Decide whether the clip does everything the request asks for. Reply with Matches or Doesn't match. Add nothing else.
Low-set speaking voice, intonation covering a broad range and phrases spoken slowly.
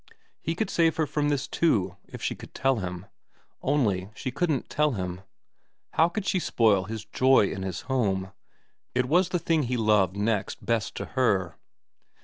Doesn't match